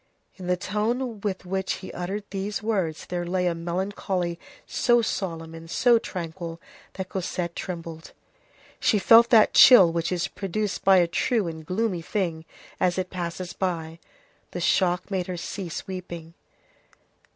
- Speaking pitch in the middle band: Yes, medium, 180 Hz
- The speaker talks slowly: No, average, 150 wpm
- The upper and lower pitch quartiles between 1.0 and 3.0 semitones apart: Yes, average, 2.7 semitones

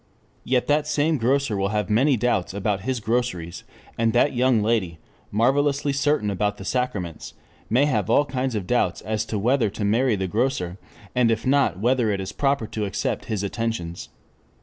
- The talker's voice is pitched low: Yes, low, 115 Hz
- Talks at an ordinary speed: Yes, average, 180 wpm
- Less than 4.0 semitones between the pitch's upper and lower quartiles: No, average, 4.3 semitones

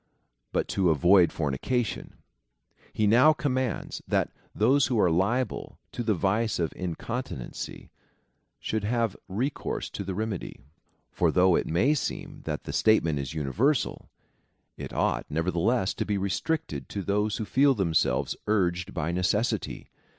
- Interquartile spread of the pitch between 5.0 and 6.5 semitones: Yes, wide, 5.4 semitones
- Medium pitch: No, low, 100 Hz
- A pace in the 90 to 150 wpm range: Yes, average, 140 wpm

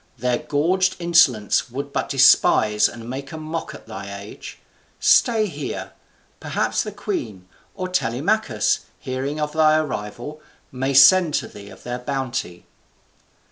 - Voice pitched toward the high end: No, medium, 140 Hz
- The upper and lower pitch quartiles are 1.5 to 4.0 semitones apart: No, average, 5.2 semitones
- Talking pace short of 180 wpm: Yes, average, 140 wpm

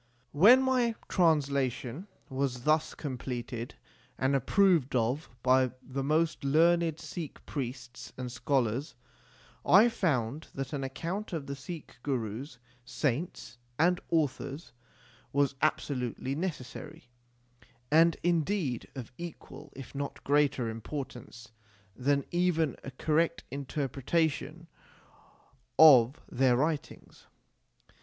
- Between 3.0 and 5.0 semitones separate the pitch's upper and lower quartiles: Yes, average, 4.1 semitones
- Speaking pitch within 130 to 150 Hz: Yes, medium, 140 Hz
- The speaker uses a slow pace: Yes, slow, 105 wpm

